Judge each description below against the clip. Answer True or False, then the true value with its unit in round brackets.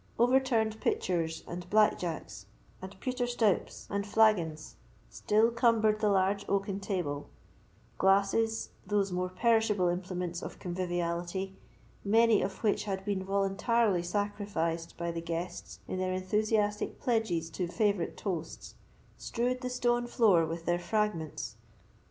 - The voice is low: False (195 Hz)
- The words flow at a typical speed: False (130 wpm)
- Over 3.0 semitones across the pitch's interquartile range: True (3.8 semitones)